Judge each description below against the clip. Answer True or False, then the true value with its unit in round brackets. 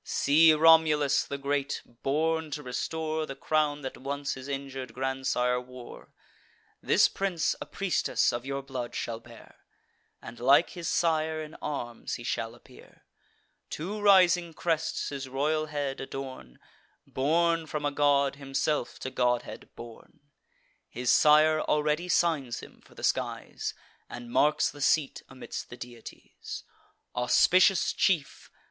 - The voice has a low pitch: False (145 Hz)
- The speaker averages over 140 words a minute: False (135 wpm)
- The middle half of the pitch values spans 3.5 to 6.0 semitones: False (3.1 semitones)